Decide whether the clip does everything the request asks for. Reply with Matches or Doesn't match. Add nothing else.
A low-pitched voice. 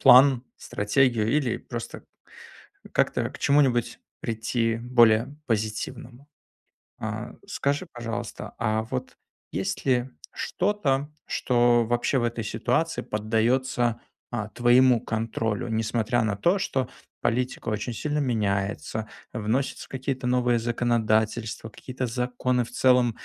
Matches